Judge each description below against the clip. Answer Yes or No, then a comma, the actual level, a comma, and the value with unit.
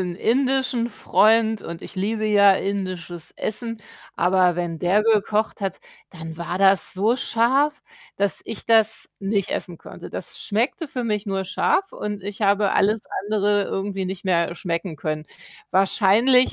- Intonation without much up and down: No, average, 3.2 semitones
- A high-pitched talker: Yes, high, 200 Hz